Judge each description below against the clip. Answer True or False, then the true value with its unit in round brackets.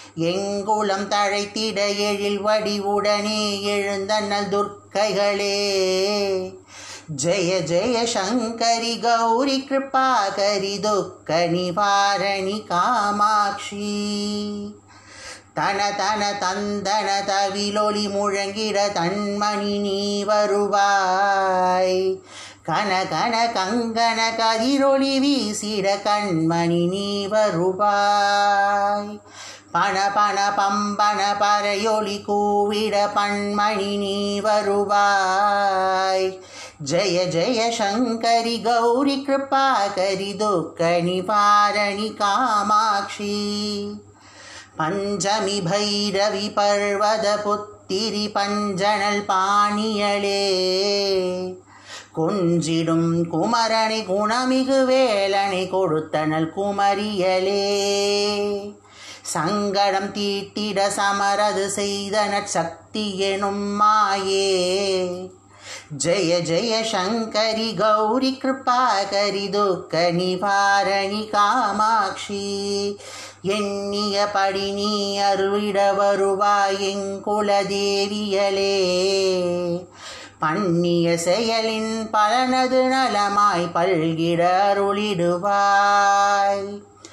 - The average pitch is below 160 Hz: False (205 Hz)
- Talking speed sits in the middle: False (55 wpm)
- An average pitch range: False (1.2 semitones)